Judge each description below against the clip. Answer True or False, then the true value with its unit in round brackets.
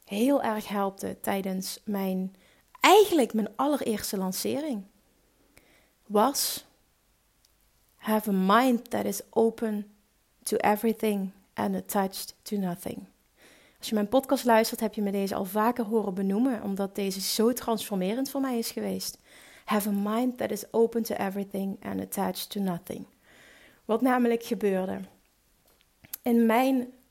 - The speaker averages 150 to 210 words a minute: False (135 wpm)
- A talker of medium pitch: False (215 Hz)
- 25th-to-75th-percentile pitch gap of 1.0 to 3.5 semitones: True (3.2 semitones)